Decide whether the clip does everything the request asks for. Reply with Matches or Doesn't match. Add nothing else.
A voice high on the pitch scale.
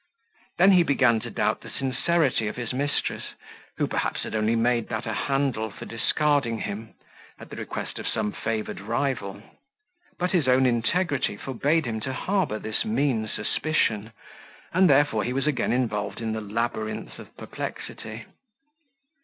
Doesn't match